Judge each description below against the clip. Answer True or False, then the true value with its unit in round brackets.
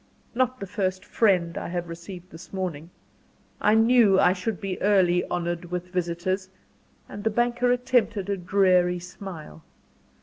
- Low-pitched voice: False (185 Hz)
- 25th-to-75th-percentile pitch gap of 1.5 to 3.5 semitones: True (2.8 semitones)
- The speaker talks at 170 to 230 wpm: False (145 wpm)